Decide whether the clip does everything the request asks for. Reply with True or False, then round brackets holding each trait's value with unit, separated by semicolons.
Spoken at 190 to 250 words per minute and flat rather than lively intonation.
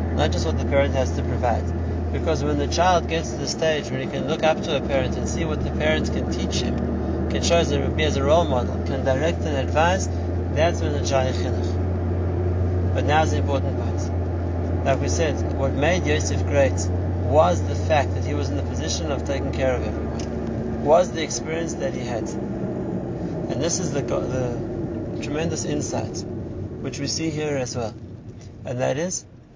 True (195 wpm; 2.1 semitones)